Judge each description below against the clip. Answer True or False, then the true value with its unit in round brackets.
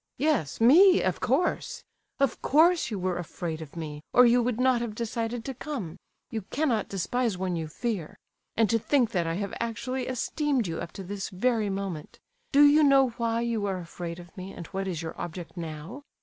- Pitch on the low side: False (220 Hz)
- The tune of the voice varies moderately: False (6.2 semitones)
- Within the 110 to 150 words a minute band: False (200 wpm)